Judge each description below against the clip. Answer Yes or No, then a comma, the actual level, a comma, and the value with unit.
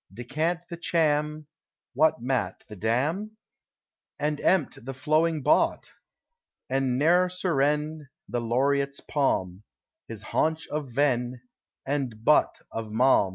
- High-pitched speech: No, medium, 140 Hz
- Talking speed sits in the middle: No, slow, 115 wpm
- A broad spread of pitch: No, average, 4.2 semitones